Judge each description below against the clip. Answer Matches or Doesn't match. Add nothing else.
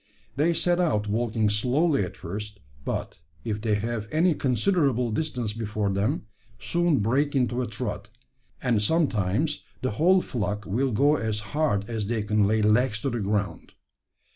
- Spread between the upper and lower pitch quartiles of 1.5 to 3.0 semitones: Doesn't match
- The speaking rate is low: Doesn't match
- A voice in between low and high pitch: Doesn't match